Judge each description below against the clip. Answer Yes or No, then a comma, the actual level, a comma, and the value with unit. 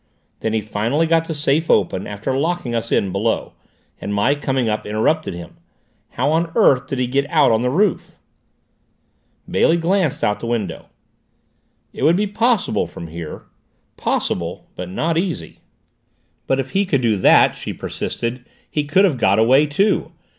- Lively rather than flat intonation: Yes, wide, 6.8 semitones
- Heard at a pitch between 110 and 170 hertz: Yes, low, 135 Hz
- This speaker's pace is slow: No, average, 170 wpm